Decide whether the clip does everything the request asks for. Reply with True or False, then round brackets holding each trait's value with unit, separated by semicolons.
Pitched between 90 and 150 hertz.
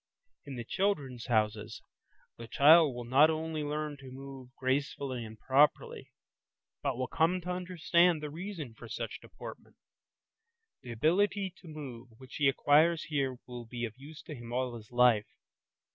True (140 Hz)